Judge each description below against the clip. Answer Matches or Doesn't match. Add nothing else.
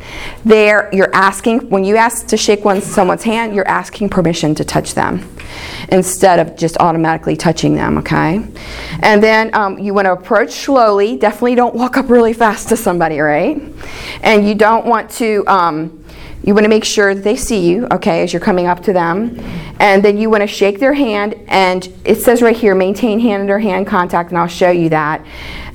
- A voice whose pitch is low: Doesn't match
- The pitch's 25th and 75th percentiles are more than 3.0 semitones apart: Matches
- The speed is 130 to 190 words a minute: Doesn't match